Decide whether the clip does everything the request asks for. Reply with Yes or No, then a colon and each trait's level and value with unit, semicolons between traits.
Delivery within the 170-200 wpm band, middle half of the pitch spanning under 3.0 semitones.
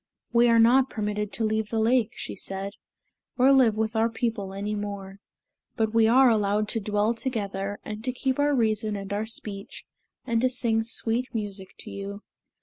Yes: average, 185 wpm; narrow, 2.4 semitones